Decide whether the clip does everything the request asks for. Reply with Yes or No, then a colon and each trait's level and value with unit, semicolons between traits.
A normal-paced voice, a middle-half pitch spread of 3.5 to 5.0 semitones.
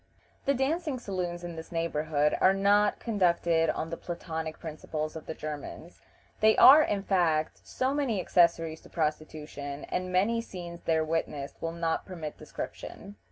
Yes: average, 155 wpm; average, 3.9 semitones